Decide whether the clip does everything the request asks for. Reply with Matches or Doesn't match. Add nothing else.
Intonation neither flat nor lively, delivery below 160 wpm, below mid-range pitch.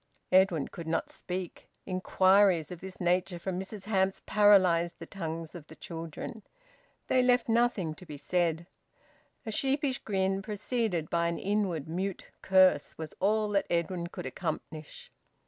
Doesn't match